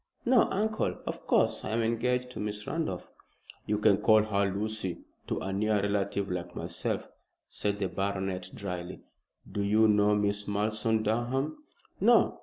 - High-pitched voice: No, low, 105 Hz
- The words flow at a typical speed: Yes, average, 155 wpm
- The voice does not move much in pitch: Yes, narrow, 1.9 semitones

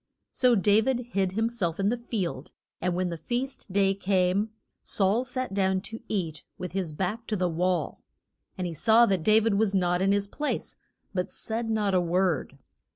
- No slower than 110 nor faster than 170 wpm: No, average, 195 wpm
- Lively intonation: No, average, 3.6 semitones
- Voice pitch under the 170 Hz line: No, high, 195 Hz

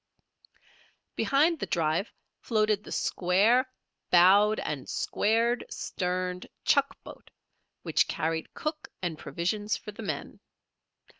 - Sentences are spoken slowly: Yes, slow, 105 wpm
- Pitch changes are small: No, average, 4.1 semitones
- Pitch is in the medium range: No, high, 205 Hz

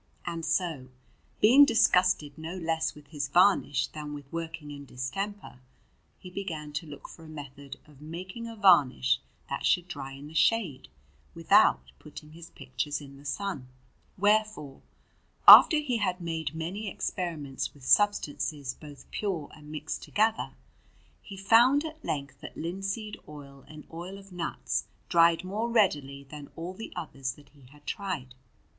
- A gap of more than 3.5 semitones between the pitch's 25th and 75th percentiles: Yes, average, 5.2 semitones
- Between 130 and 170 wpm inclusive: Yes, average, 155 wpm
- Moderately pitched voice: Yes, medium, 160 Hz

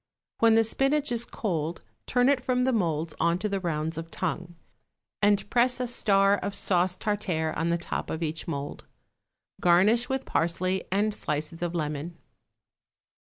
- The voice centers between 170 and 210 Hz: Yes, medium, 185 Hz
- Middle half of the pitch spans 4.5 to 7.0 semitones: Yes, wide, 5.4 semitones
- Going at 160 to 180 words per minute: Yes, average, 165 wpm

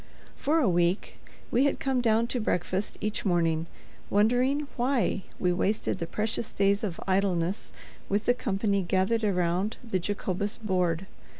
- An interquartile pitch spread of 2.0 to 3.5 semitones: No, average, 4.0 semitones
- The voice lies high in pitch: Yes, high, 200 Hz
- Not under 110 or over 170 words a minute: Yes, average, 145 wpm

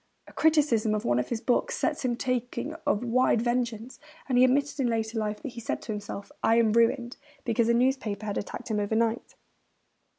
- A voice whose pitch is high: Yes, high, 235 Hz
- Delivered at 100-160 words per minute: No, average, 200 wpm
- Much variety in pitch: No, narrow, 2.5 semitones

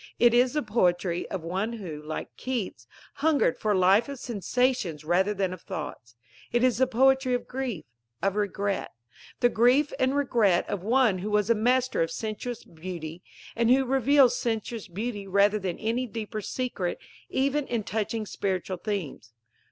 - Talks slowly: No, average, 165 wpm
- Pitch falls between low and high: No, high, 215 Hz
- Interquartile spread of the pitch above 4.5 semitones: Yes, average, 5.0 semitones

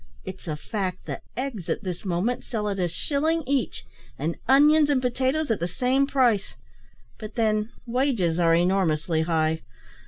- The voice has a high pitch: Yes, high, 215 Hz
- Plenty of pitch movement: Yes, wide, 7.1 semitones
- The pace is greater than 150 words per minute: Yes, average, 160 wpm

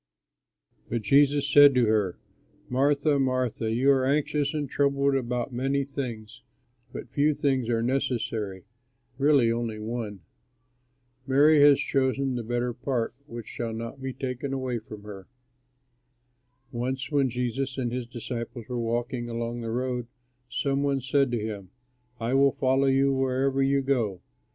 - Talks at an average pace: Yes, average, 145 wpm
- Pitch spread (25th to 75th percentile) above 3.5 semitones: No, average, 2.7 semitones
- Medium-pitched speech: No, low, 130 Hz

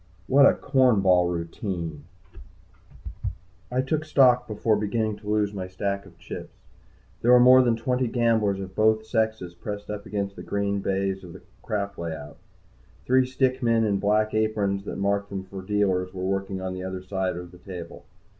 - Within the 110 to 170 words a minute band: No, average, 180 wpm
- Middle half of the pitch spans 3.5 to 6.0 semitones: No, average, 3.0 semitones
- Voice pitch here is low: Yes, low, 100 Hz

